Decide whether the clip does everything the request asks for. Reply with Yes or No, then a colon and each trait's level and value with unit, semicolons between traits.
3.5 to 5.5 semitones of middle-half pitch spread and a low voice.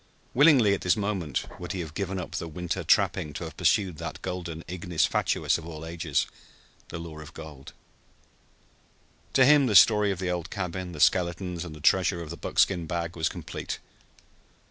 No: average, 2.8 semitones; very low, 90 Hz